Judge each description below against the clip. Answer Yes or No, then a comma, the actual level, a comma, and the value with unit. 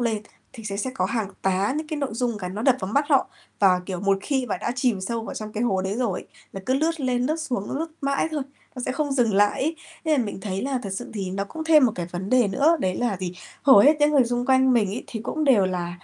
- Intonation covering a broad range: Yes, wide, 5.7 semitones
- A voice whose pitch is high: Yes, high, 240 Hz